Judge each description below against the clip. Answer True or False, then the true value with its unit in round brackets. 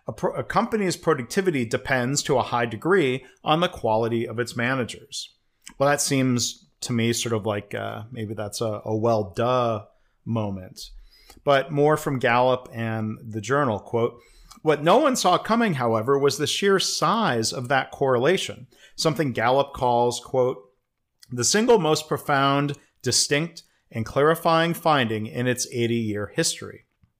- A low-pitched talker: True (125 Hz)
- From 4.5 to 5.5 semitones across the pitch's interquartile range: True (4.9 semitones)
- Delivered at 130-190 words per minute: True (150 wpm)